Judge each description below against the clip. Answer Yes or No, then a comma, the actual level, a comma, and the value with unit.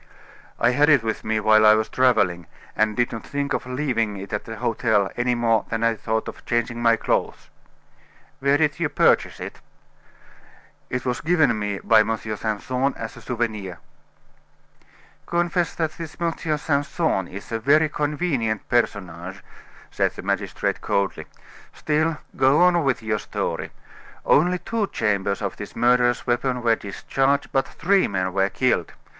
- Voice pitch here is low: Yes, low, 120 Hz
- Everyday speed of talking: Yes, average, 160 wpm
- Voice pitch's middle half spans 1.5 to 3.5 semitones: No, average, 4.8 semitones